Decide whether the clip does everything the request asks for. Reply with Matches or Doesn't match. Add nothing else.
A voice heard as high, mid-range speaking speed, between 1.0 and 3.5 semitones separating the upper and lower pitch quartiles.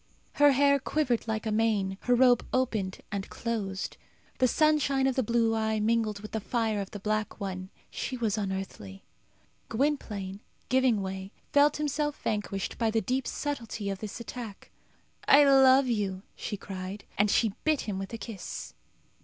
Doesn't match